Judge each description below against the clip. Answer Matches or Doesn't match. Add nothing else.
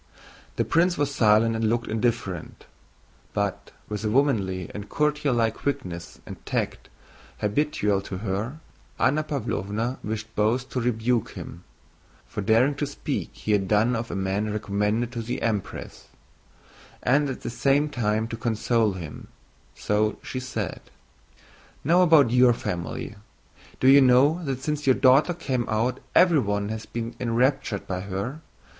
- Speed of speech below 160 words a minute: Matches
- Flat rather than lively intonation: Doesn't match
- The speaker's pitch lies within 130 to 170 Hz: Doesn't match